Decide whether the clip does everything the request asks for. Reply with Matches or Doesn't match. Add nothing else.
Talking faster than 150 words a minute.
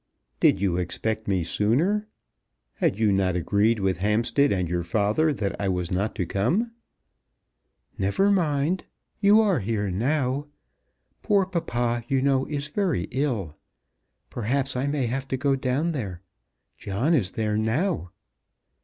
Doesn't match